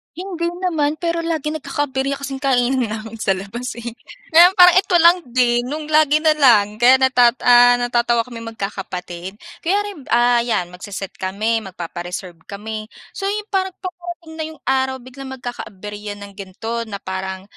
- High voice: Yes, high, 245 Hz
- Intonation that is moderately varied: No, wide, 6.5 semitones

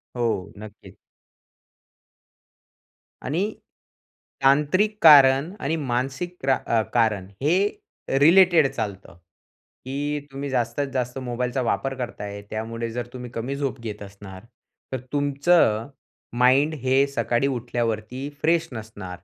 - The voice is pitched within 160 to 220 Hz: No, low, 130 Hz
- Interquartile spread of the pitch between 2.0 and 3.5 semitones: No, average, 3.9 semitones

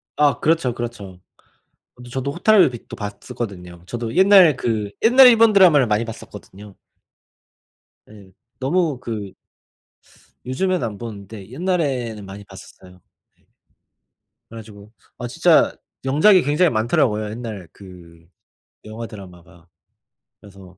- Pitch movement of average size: No, wide, 6.4 semitones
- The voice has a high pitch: No, low, 115 Hz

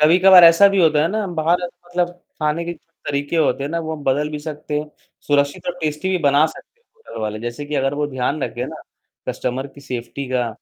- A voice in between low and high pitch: Yes, medium, 150 Hz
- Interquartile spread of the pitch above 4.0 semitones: No, average, 3.1 semitones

